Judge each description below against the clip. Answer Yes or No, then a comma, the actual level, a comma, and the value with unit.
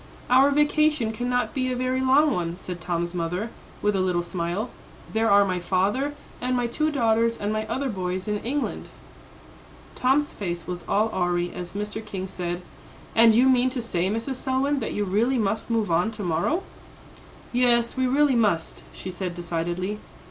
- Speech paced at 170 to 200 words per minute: Yes, average, 175 wpm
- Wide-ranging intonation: Yes, wide, 5.9 semitones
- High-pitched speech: Yes, high, 215 Hz